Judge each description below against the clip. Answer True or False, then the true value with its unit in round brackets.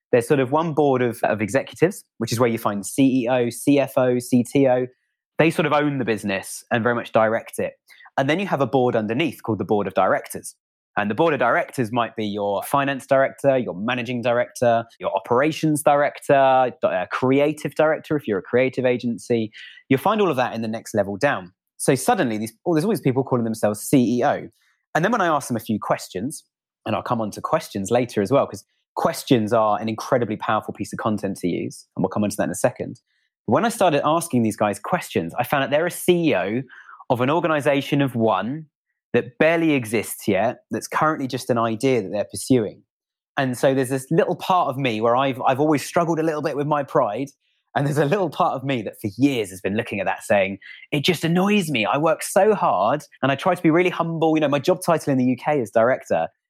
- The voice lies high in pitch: False (135 Hz)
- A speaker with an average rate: False (225 wpm)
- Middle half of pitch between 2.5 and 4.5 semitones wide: False (5.0 semitones)